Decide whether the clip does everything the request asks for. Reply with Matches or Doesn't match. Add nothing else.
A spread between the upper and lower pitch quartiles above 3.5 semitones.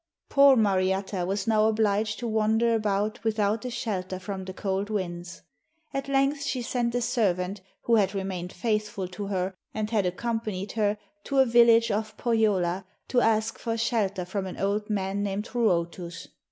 Doesn't match